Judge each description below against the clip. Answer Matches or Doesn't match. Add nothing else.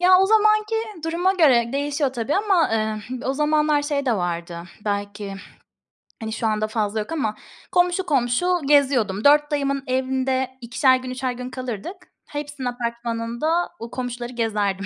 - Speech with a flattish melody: Doesn't match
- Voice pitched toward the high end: Matches